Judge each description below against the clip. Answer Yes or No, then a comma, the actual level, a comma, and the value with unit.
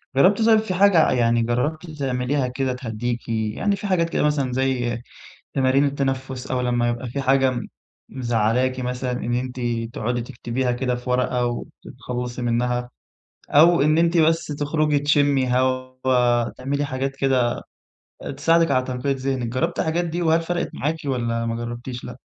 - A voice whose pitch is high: No, low, 130 Hz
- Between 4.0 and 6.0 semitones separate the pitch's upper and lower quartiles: No, average, 2.9 semitones